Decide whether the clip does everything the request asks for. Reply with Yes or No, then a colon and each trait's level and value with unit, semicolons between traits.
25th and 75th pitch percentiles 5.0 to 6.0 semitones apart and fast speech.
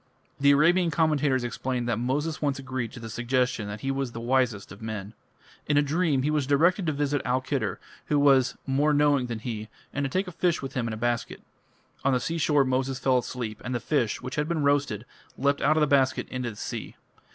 No: average, 3.3 semitones; fast, 225 wpm